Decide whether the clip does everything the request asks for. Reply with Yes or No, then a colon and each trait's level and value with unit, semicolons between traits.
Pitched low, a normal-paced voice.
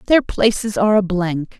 No: high, 195 Hz; average, 190 wpm